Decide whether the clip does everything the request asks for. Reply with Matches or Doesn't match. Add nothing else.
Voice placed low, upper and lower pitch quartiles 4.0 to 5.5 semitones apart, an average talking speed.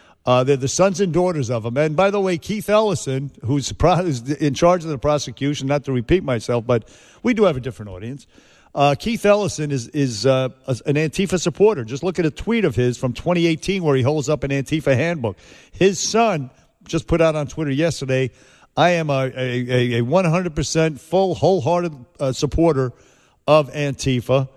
Doesn't match